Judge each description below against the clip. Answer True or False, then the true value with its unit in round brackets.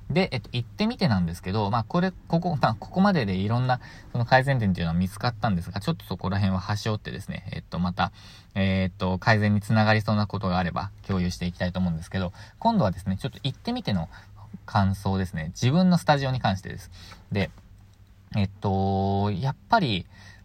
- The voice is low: True (100 Hz)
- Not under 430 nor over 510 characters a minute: True (440 characters per minute)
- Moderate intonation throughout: True (4.4 semitones)